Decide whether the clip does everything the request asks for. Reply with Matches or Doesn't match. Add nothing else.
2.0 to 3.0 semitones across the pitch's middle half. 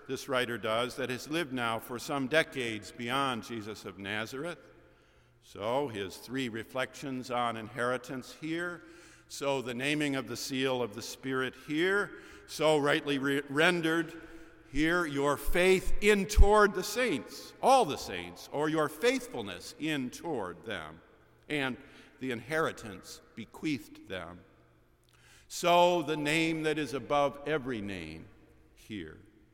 Doesn't match